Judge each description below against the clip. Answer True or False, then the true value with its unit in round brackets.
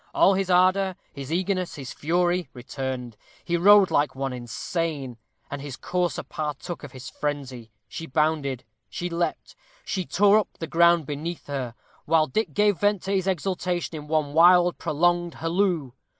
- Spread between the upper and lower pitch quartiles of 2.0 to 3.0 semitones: False (4.1 semitones)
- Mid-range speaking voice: True (165 Hz)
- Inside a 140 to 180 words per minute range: True (160 wpm)